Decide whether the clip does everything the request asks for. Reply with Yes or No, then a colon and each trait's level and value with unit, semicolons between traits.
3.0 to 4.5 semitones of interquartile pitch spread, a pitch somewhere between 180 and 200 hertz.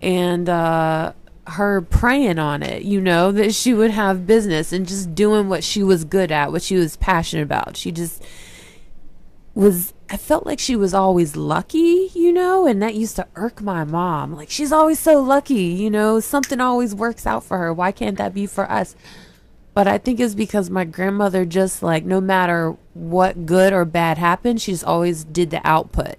Yes: average, 4.2 semitones; high, 190 Hz